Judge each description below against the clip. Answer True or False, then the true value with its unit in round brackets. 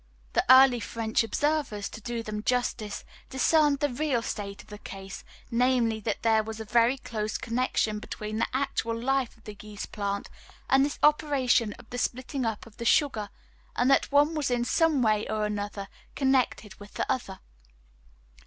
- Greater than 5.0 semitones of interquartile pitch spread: False (3.9 semitones)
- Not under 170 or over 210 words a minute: True (175 wpm)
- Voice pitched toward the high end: True (235 Hz)